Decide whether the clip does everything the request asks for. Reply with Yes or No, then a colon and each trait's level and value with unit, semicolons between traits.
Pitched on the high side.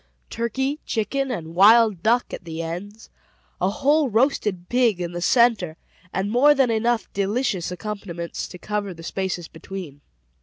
Yes: high, 205 Hz